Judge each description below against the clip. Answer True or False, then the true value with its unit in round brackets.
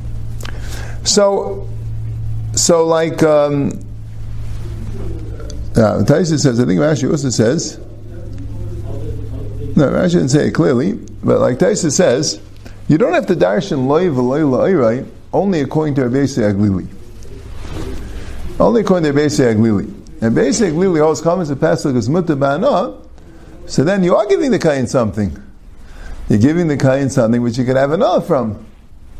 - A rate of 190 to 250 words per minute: False (140 wpm)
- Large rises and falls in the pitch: True (5.7 semitones)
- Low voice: True (115 Hz)